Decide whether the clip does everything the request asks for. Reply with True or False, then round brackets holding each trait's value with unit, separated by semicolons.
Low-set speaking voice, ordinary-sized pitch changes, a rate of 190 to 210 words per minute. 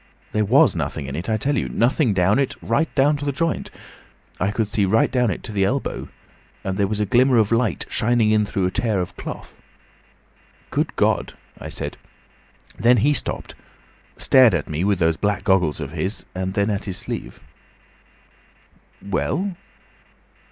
False (105 Hz; 4.5 semitones; 180 wpm)